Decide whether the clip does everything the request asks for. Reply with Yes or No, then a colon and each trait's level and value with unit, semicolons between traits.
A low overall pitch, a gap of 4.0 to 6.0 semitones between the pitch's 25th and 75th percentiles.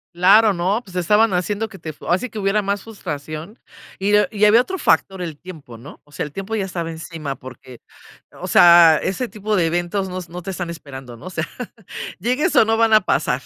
No: medium, 185 Hz; average, 4.4 semitones